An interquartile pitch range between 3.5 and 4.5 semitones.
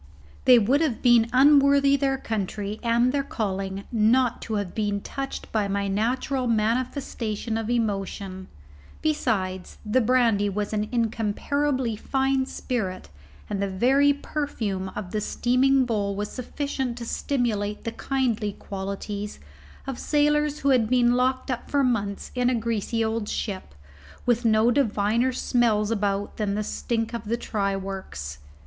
Yes: average, 3.9 semitones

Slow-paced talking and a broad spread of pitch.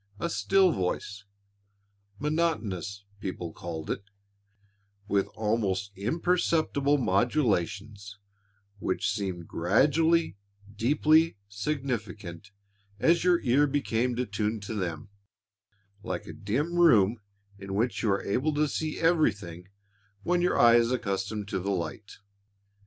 Yes: slow, 115 wpm; wide, 7.0 semitones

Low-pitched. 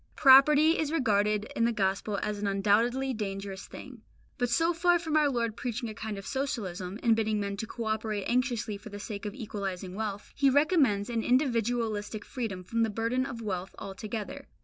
No: high, 220 Hz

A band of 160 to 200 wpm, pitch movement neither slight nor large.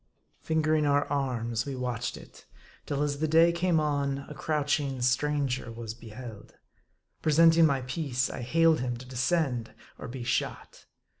No: average, 150 wpm; average, 3.8 semitones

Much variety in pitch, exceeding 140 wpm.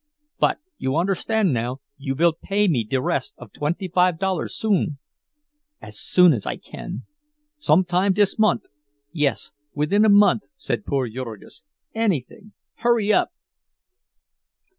No: wide, 6.8 semitones; slow, 135 wpm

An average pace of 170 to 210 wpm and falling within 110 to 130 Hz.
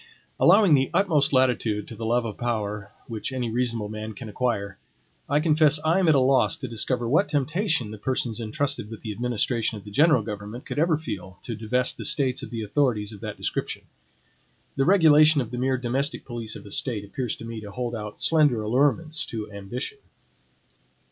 Yes: average, 195 wpm; low, 120 Hz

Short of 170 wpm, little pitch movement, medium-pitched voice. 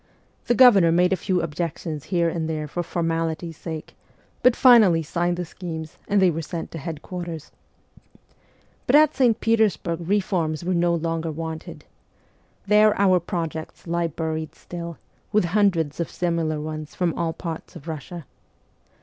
Yes: average, 150 wpm; narrow, 2.3 semitones; medium, 170 Hz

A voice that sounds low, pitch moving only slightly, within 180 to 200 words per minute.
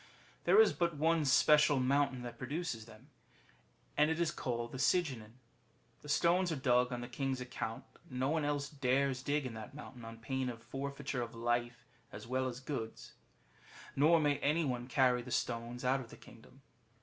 No: low, 130 Hz; average, 3.3 semitones; average, 185 wpm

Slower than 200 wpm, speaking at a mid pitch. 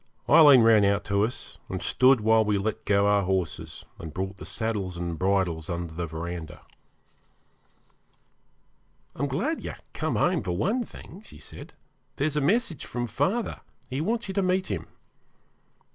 No: average, 165 wpm; low, 110 Hz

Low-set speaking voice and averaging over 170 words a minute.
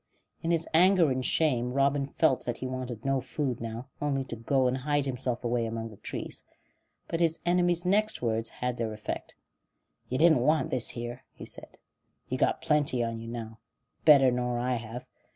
Yes: low, 130 Hz; average, 190 wpm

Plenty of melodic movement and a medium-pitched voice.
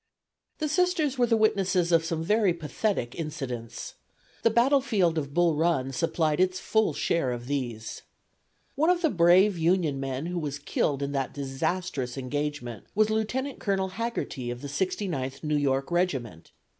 Yes: wide, 7.1 semitones; medium, 165 Hz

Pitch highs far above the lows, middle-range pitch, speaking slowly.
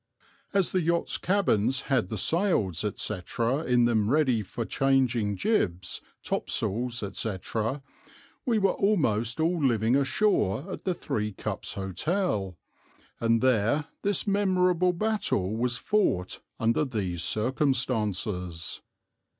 No: wide, 8.3 semitones; low, 125 Hz; slow, 120 wpm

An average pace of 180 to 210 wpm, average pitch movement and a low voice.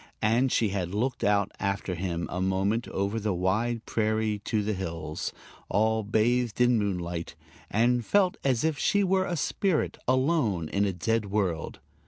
No: average, 165 wpm; average, 4.3 semitones; low, 110 Hz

